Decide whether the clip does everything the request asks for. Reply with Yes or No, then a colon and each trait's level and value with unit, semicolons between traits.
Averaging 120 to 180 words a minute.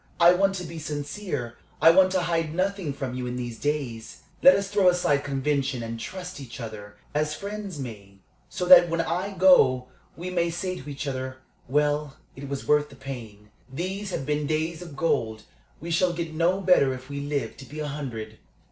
No: average, 200 wpm